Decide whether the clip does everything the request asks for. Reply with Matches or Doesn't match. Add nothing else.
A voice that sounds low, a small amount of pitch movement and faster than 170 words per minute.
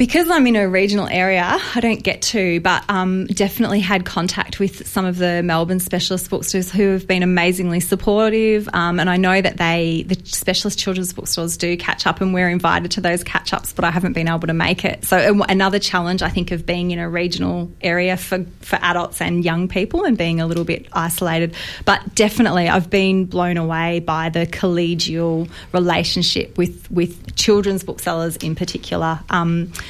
Doesn't match